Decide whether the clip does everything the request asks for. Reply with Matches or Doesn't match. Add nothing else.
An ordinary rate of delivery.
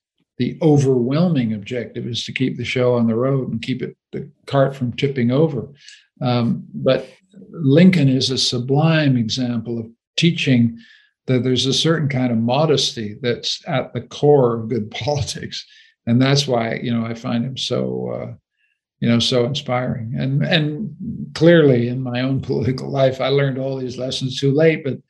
Matches